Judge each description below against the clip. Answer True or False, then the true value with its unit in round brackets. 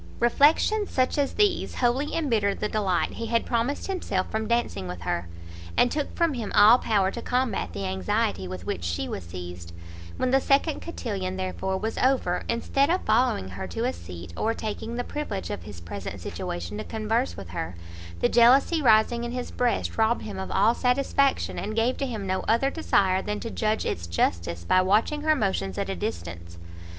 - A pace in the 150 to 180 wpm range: False (195 wpm)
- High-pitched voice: True (215 Hz)